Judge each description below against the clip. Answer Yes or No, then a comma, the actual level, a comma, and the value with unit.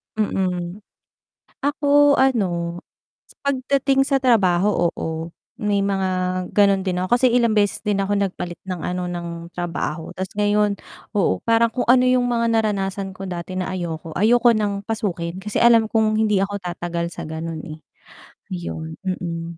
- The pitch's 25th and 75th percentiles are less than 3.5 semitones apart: No, average, 4.5 semitones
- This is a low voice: No, high, 195 Hz